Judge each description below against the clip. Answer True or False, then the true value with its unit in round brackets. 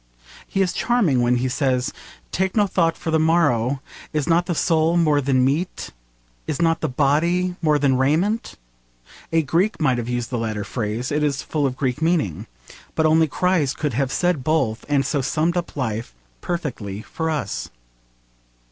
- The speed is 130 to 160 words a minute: False (175 wpm)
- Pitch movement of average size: True (4.6 semitones)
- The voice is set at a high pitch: False (150 Hz)